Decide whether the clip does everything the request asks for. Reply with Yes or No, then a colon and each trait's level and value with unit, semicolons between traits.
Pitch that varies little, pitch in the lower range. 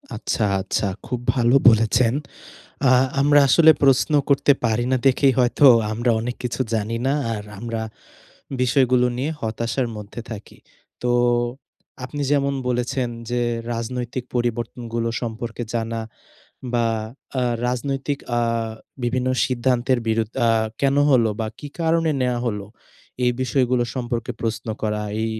Yes: narrow, 2.1 semitones; low, 120 Hz